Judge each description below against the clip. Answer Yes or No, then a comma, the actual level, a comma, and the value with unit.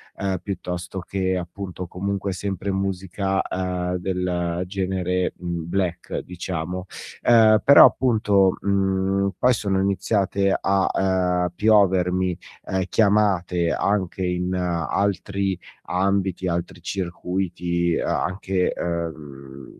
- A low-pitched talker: Yes, very low, 95 Hz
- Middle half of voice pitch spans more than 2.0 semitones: No, narrow, 1.7 semitones